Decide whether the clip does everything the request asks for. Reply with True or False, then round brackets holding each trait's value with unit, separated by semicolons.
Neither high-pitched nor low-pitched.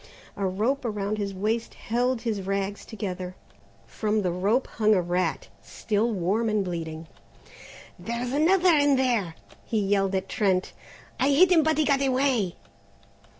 False (215 Hz)